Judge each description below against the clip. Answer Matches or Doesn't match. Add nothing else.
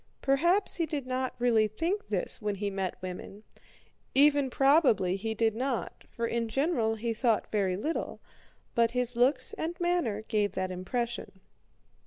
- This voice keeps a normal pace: Matches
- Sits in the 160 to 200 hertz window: Doesn't match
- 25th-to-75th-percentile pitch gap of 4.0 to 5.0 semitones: Matches